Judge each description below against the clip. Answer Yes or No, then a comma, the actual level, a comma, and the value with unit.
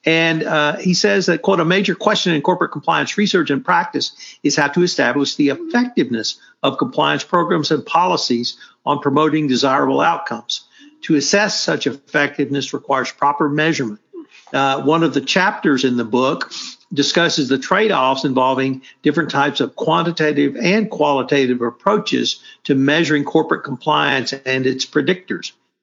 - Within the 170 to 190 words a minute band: No, average, 145 wpm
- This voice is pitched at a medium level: Yes, medium, 150 Hz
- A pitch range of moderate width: Yes, average, 4.2 semitones